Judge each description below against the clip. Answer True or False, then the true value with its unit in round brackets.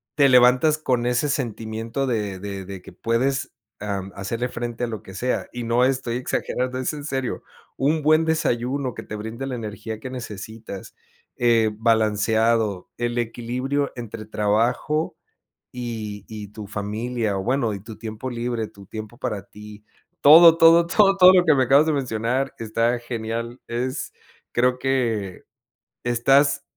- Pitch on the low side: True (120 Hz)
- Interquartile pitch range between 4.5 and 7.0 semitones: False (3.3 semitones)